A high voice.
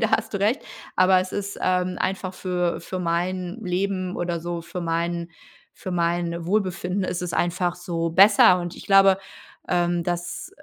No: medium, 180 Hz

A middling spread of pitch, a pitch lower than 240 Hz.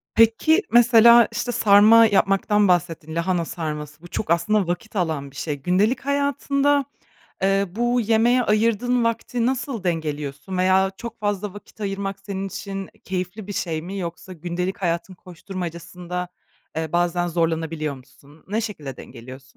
Yes: average, 4.9 semitones; high, 190 Hz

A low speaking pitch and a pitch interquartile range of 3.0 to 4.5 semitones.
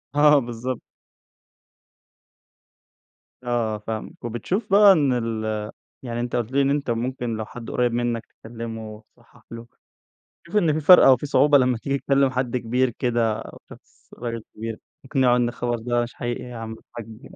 No: low, 120 Hz; narrow, 2.6 semitones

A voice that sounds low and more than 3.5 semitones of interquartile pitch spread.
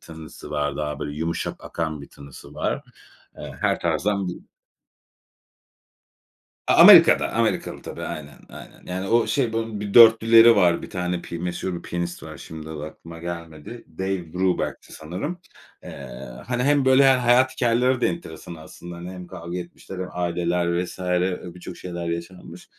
Yes: very low, 90 Hz; average, 3.9 semitones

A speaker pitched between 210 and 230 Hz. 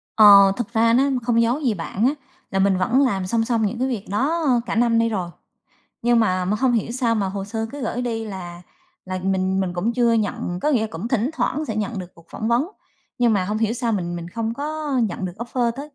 Yes: high, 225 Hz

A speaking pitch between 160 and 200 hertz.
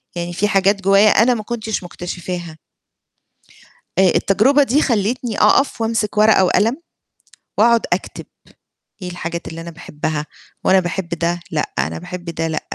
Yes: high, 190 Hz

